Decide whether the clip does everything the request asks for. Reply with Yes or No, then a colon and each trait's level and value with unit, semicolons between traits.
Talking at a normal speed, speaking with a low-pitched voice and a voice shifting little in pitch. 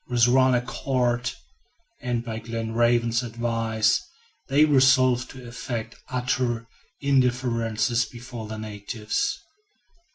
No: slow, 95 wpm; low, 120 Hz; narrow, 1.9 semitones